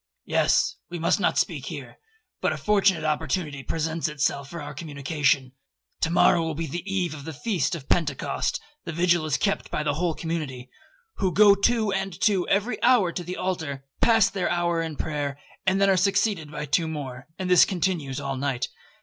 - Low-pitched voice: No, medium, 165 Hz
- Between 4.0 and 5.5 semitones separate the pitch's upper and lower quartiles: Yes, average, 4.3 semitones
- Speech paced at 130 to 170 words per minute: No, average, 190 wpm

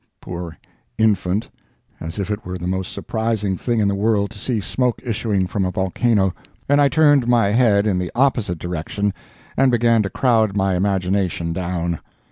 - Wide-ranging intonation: No, average, 3.9 semitones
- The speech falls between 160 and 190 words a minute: Yes, average, 170 wpm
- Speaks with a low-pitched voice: Yes, low, 100 Hz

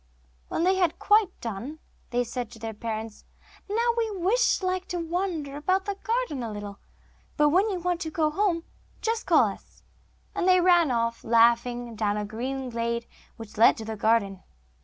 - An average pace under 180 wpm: No, average, 185 wpm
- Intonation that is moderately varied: No, wide, 8.3 semitones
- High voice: Yes, very high, 285 Hz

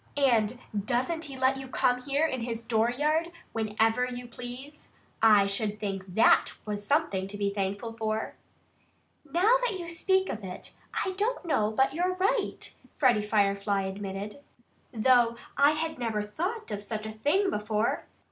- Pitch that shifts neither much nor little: No, wide, 6.3 semitones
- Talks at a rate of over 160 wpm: No, average, 155 wpm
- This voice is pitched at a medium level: No, high, 240 Hz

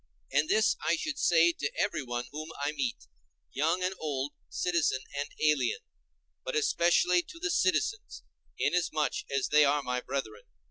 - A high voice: No, medium, 150 Hz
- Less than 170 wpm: Yes, average, 150 wpm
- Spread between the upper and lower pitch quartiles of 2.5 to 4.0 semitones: No, average, 4.5 semitones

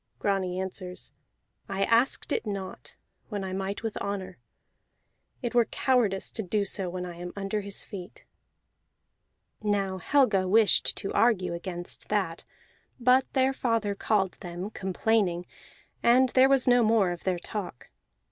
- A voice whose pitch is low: No, high, 200 Hz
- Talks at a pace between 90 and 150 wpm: Yes, average, 145 wpm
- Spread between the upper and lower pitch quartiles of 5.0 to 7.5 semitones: No, average, 3.4 semitones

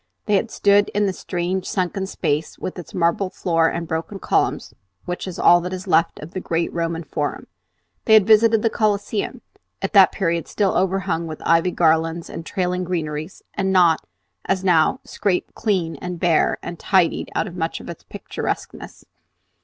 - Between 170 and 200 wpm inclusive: Yes, average, 175 wpm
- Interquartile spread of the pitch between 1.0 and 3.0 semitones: Yes, average, 2.7 semitones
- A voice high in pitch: No, medium, 180 Hz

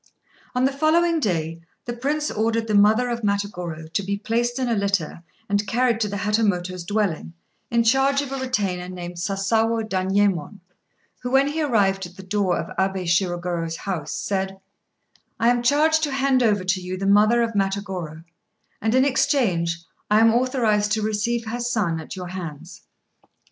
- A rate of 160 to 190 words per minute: Yes, average, 175 wpm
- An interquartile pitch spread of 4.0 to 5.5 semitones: Yes, average, 4.6 semitones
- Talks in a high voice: Yes, high, 205 Hz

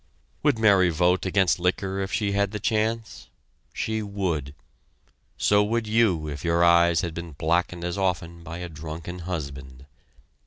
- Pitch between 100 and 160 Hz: No, very low, 90 Hz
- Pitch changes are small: No, average, 3.3 semitones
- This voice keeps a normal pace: Yes, average, 155 wpm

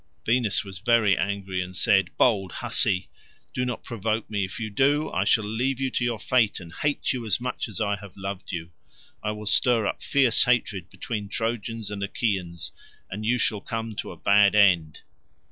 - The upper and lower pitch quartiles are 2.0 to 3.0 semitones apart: No, average, 3.4 semitones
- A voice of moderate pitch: No, low, 105 Hz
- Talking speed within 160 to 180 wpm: No, average, 195 wpm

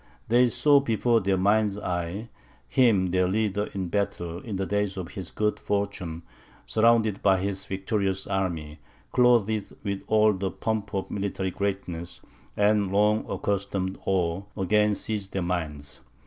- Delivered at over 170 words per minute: No, average, 145 wpm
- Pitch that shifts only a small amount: Yes, narrow, 2.3 semitones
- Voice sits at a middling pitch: No, low, 100 Hz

